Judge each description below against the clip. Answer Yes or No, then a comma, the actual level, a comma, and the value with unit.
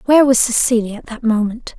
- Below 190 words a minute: No, average, 200 wpm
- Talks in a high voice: Yes, high, 235 Hz